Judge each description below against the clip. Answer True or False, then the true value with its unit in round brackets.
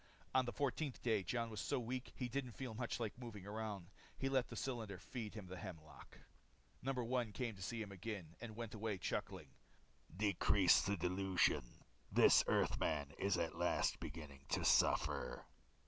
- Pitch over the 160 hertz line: False (110 Hz)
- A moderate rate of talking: True (170 wpm)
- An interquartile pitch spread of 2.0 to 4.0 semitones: False (4.4 semitones)